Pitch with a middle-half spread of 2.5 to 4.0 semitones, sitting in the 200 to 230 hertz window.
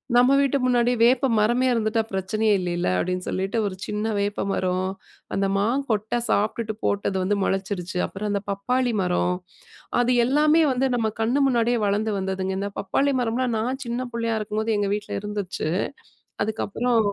Yes: average, 3.6 semitones; high, 215 Hz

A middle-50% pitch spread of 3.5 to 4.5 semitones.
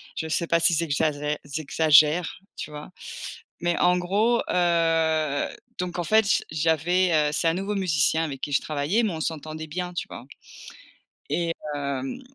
No: average, 2.9 semitones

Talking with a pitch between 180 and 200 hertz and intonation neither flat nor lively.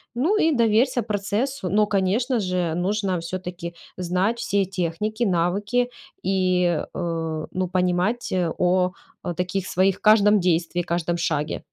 Yes: medium, 185 Hz; average, 3.2 semitones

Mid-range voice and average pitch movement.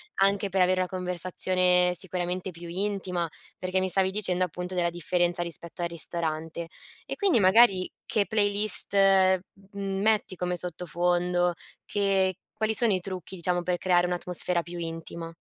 No: medium, 180 Hz; narrow, 1.7 semitones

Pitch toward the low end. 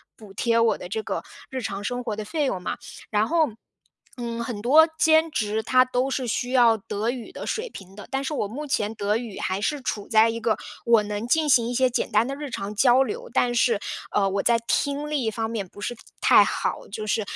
No: high, 235 Hz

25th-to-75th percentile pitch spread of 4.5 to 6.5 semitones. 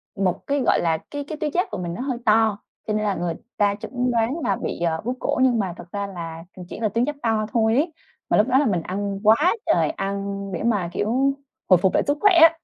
Yes: average, 5.3 semitones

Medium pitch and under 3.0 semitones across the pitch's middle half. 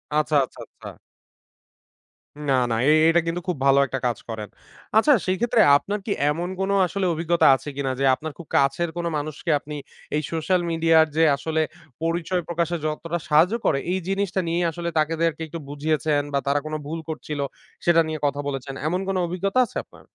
Yes: medium, 165 Hz; narrow, 2.6 semitones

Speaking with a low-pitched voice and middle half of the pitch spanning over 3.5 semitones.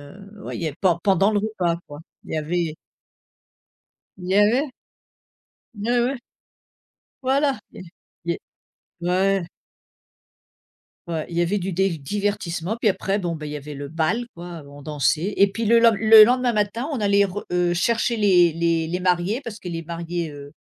No: medium, 180 Hz; average, 4.2 semitones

